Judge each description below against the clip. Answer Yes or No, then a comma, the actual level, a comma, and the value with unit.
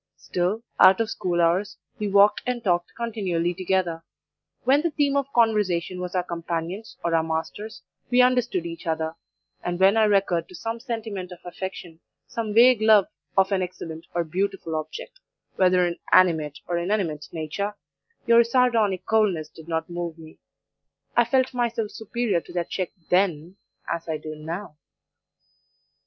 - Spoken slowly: No, average, 160 wpm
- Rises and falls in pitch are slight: No, average, 4.6 semitones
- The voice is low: No, medium, 185 Hz